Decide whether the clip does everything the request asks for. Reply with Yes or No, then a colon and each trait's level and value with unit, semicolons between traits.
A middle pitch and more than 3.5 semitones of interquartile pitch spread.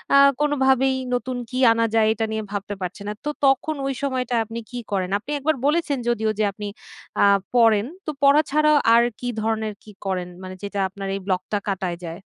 No: high, 225 Hz; average, 4.8 semitones